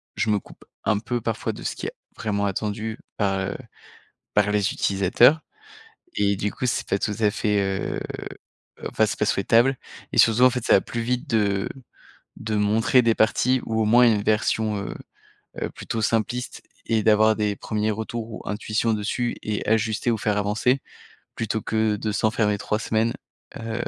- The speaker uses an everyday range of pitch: No, narrow, 1.7 semitones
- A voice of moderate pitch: No, low, 110 Hz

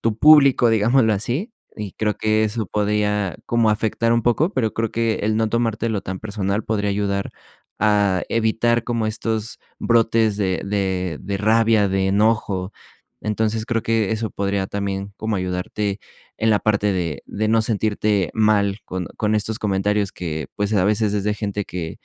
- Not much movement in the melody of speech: Yes, narrow, 2.1 semitones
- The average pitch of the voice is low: Yes, low, 105 Hz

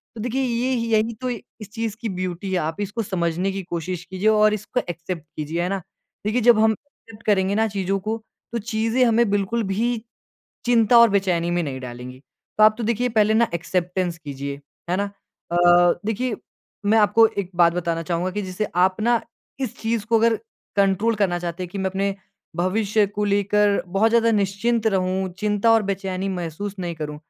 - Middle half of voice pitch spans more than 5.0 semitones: No, average, 3.7 semitones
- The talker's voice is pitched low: No, high, 200 Hz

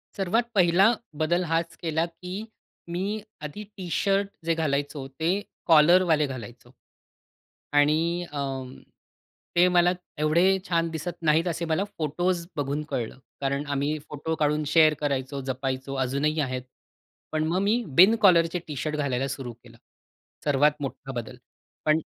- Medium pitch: Yes, medium, 155 Hz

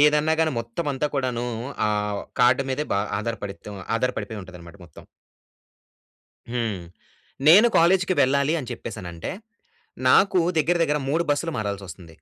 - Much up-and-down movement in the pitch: Yes, wide, 6.7 semitones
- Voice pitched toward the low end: Yes, low, 125 Hz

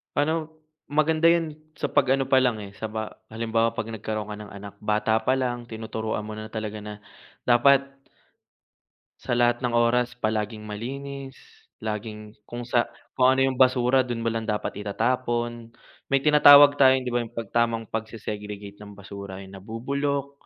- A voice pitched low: Yes, low, 115 Hz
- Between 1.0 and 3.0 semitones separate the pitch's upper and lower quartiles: No, average, 3.5 semitones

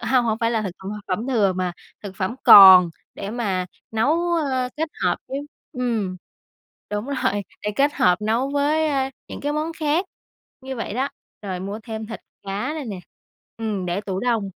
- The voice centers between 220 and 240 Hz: Yes, high, 225 Hz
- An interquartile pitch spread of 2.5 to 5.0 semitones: No, wide, 5.6 semitones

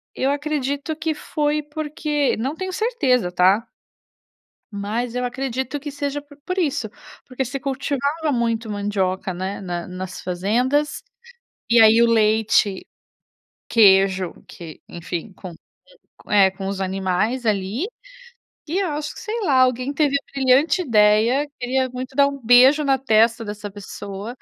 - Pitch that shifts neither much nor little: No, wide, 5.9 semitones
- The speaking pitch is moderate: No, high, 245 Hz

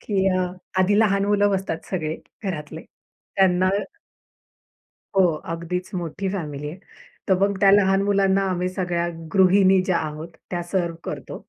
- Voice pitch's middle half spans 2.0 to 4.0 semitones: Yes, narrow, 2.4 semitones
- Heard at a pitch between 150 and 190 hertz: Yes, medium, 185 Hz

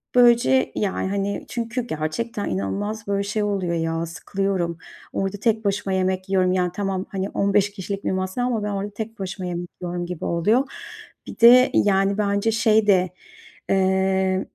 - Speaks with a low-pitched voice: No, high, 195 Hz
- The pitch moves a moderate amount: No, narrow, 2.2 semitones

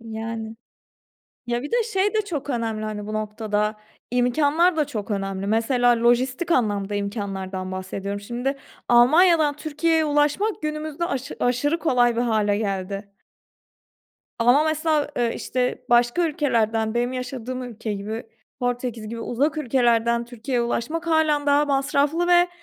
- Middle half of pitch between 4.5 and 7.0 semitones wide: Yes, average, 5.1 semitones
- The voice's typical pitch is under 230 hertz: No, high, 245 Hz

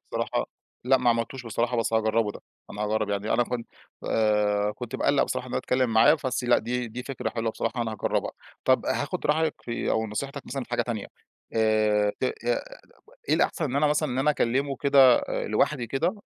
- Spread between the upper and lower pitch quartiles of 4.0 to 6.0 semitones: No, average, 3.3 semitones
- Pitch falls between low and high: No, low, 120 Hz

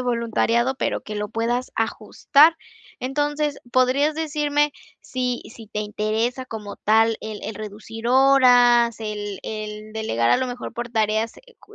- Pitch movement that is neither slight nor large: Yes, average, 3.2 semitones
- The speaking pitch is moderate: No, high, 235 Hz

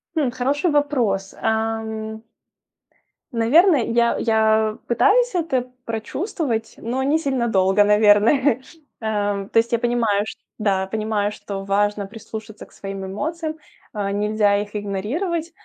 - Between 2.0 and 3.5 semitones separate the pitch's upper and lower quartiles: No, average, 4.1 semitones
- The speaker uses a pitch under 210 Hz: No, high, 220 Hz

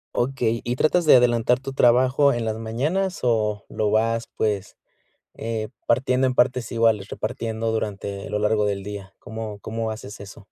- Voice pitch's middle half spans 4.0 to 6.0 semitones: No, average, 2.8 semitones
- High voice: No, low, 115 Hz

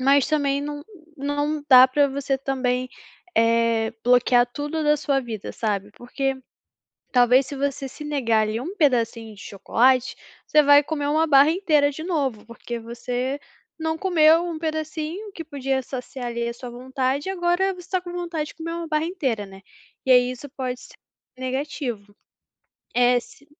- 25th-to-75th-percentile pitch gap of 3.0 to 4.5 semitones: Yes, average, 3.8 semitones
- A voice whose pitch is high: Yes, very high, 275 Hz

